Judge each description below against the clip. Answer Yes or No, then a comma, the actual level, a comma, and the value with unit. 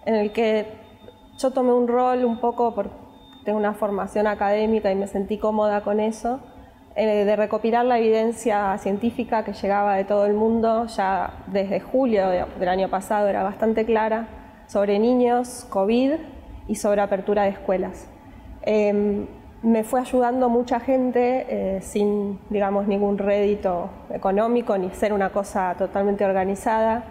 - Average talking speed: Yes, average, 150 wpm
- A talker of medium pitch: No, high, 215 Hz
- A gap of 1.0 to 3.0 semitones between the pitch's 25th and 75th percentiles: Yes, narrow, 2.5 semitones